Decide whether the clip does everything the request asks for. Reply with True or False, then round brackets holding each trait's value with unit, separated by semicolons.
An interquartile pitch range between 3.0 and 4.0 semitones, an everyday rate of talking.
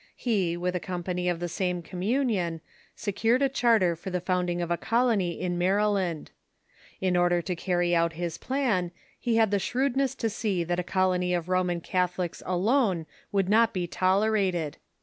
True (3.3 semitones; 170 wpm)